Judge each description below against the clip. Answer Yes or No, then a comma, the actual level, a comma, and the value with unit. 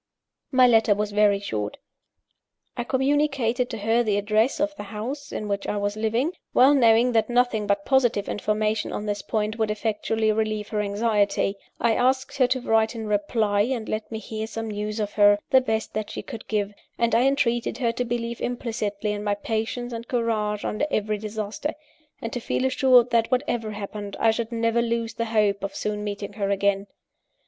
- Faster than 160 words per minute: Yes, average, 190 wpm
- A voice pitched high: Yes, high, 220 Hz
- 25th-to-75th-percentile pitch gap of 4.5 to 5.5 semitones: No, narrow, 2.4 semitones